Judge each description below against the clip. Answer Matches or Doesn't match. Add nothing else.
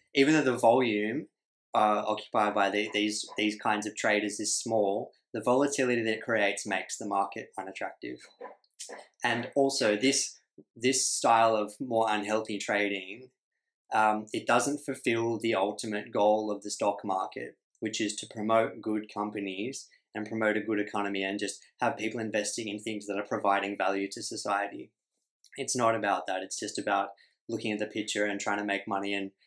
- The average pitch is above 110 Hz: Doesn't match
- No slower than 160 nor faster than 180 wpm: Matches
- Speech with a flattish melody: Matches